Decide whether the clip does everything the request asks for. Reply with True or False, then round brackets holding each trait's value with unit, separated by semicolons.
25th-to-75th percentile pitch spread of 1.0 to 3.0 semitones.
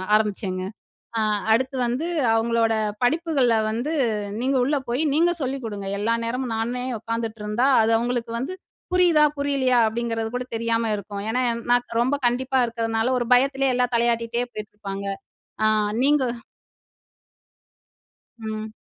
True (2.6 semitones)